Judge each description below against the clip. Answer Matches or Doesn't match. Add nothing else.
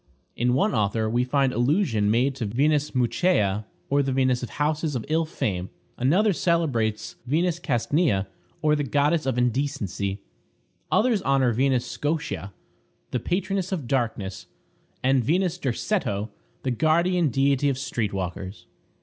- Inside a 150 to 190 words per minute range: Doesn't match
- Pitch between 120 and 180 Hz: Matches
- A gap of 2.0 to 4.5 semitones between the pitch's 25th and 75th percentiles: Doesn't match